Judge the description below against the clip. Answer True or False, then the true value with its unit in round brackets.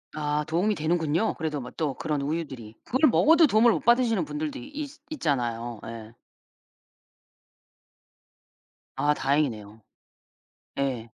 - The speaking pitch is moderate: True (150 Hz)